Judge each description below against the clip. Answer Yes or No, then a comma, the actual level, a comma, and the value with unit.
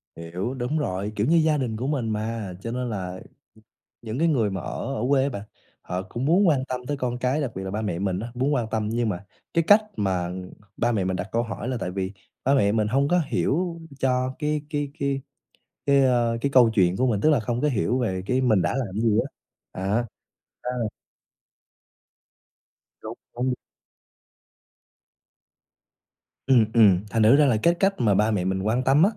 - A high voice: No, low, 120 Hz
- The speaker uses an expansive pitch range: No, average, 5.0 semitones